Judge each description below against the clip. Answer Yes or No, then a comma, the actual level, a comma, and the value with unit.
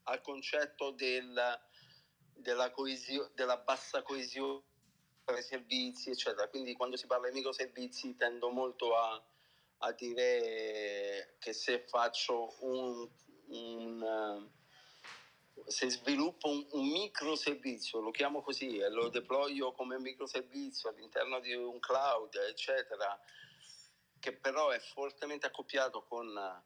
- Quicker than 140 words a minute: No, slow, 115 wpm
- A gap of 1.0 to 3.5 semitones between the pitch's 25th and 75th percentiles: Yes, average, 2.7 semitones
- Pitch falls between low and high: No, low, 130 Hz